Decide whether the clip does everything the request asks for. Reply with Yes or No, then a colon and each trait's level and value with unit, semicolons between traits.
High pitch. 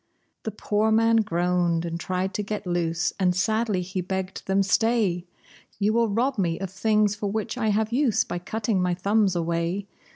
Yes: high, 195 Hz